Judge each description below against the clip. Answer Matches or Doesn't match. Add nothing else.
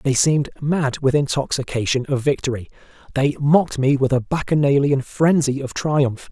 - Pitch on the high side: Doesn't match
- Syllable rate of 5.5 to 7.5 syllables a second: Doesn't match